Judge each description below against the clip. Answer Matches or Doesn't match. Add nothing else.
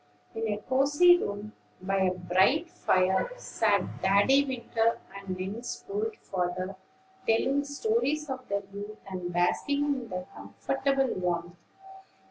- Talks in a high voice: Matches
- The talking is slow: Matches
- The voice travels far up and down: Matches